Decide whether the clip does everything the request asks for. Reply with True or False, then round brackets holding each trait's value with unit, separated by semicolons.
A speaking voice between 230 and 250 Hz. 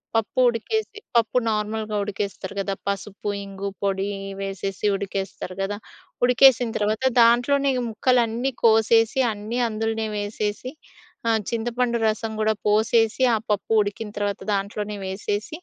False (215 Hz)